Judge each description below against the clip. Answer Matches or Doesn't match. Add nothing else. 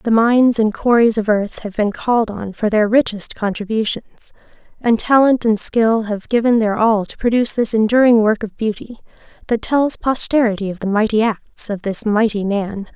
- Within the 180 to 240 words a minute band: Matches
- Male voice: Doesn't match